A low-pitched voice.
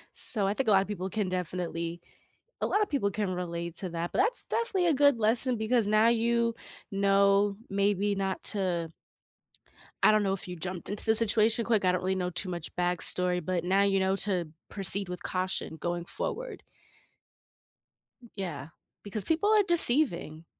No: high, 195 Hz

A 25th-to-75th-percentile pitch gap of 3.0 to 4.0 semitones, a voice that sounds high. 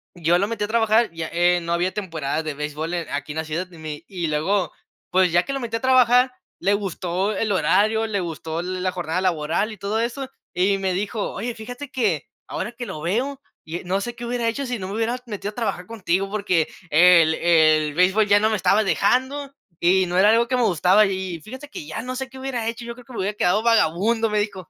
No: average, 4.9 semitones; high, 195 Hz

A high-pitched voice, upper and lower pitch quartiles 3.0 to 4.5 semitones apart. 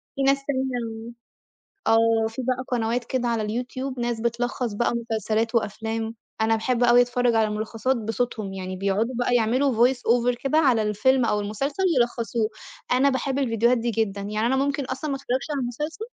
No: high, 240 Hz; narrow, 2.6 semitones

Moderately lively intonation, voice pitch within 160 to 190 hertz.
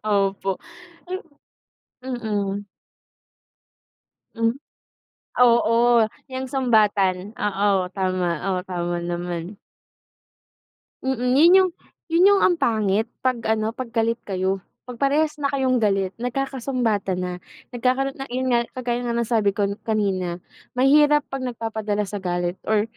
No: average, 4.7 semitones; high, 225 Hz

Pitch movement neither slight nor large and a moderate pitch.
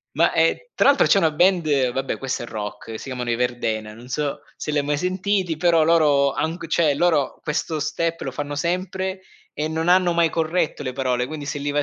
Yes: average, 4.2 semitones; medium, 150 Hz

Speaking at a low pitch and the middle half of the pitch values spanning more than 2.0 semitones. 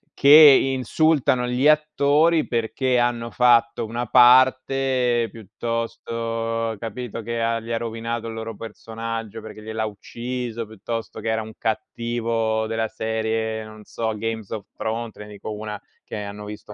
No: low, 115 Hz; narrow, 1.7 semitones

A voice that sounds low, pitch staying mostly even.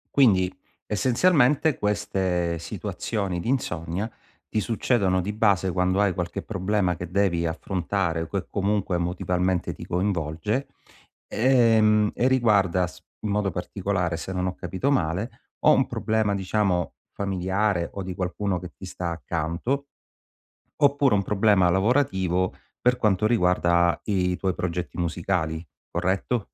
No: very low, 95 Hz; average, 3.2 semitones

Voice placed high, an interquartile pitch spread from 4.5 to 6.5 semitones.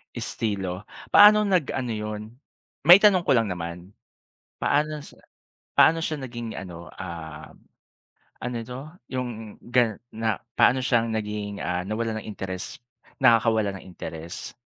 No: low, 110 Hz; average, 5.0 semitones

